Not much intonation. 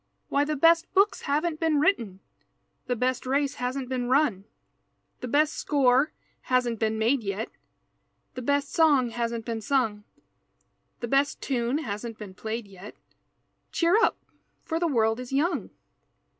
No: average, 4.2 semitones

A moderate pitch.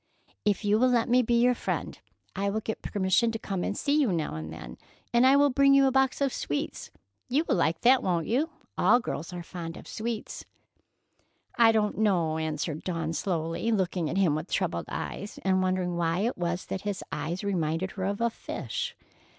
No: high, 195 Hz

